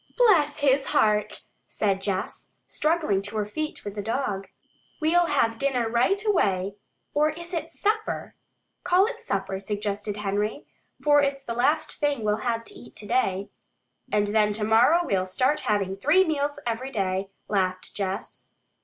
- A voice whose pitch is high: Yes, high, 230 Hz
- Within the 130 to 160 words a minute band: Yes, average, 155 wpm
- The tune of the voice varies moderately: No, wide, 6.6 semitones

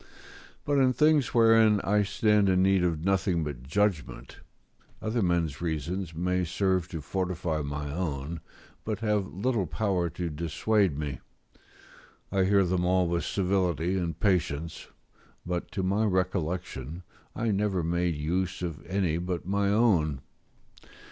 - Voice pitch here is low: Yes, very low, 90 Hz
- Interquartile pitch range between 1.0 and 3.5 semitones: Yes, average, 3.2 semitones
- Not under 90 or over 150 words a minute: Yes, average, 140 wpm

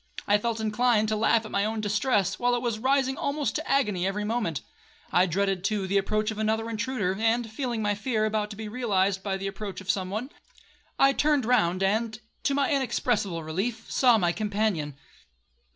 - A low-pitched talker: No, high, 215 Hz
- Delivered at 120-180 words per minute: No, average, 195 wpm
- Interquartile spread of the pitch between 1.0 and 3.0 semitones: No, average, 3.5 semitones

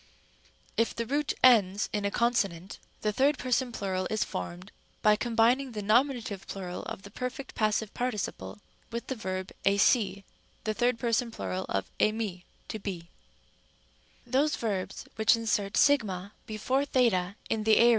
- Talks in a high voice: Yes, high, 215 Hz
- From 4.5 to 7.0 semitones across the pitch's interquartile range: No, average, 3.6 semitones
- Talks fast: No, average, 160 wpm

